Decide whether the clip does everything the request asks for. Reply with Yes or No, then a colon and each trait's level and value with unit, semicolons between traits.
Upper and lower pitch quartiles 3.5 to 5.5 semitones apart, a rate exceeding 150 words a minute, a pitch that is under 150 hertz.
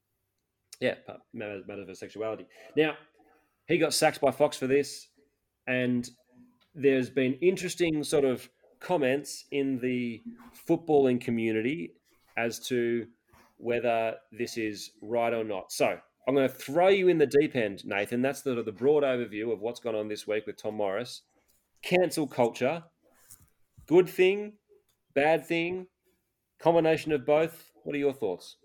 No: average, 5.1 semitones; average, 145 wpm; medium, 140 Hz